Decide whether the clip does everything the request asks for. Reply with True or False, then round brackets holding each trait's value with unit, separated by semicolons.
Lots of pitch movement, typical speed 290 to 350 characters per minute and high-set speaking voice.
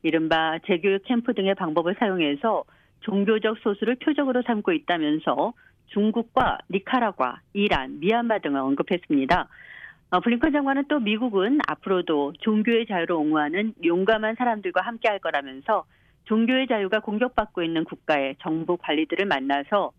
True (5.9 semitones; 345 characters per minute; 210 Hz)